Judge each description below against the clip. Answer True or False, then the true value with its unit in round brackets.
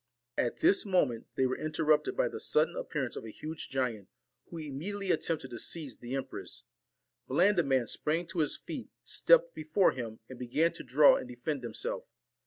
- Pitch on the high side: False (150 Hz)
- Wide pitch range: True (5.7 semitones)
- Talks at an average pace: True (185 wpm)